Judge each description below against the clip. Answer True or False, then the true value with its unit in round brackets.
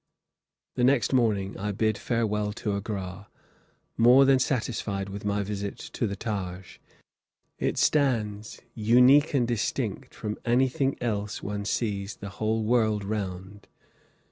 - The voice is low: True (105 Hz)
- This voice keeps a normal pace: False (130 wpm)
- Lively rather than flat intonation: False (3.0 semitones)